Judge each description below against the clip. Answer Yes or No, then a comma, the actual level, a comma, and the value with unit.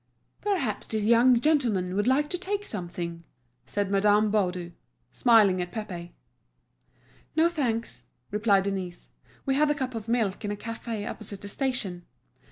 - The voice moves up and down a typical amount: Yes, average, 4.8 semitones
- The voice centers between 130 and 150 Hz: No, high, 215 Hz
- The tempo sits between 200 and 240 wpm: No, average, 150 wpm